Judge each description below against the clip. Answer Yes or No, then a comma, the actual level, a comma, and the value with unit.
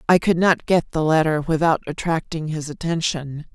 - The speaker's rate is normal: Yes, average, 170 wpm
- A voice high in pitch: No, medium, 160 Hz